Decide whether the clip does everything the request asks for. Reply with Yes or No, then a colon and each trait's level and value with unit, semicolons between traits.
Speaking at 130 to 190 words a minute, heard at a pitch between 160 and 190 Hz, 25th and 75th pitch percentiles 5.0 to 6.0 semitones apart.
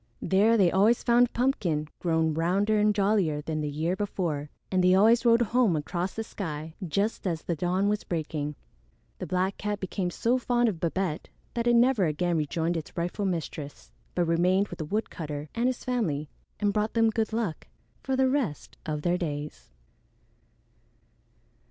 Yes: average, 170 wpm; medium, 185 Hz; average, 5.3 semitones